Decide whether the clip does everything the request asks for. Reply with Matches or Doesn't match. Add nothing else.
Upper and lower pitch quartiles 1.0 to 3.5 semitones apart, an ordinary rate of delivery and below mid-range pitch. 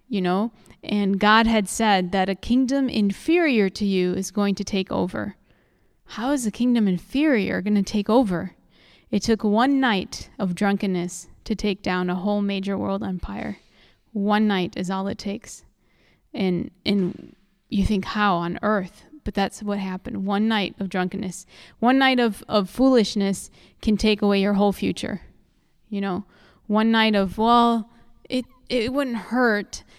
Doesn't match